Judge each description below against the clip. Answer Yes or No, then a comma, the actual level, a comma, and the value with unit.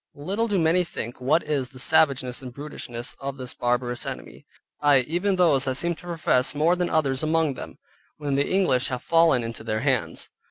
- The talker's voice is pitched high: No, medium, 140 Hz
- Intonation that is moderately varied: Yes, average, 4.5 semitones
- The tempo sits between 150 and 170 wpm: No, average, 195 wpm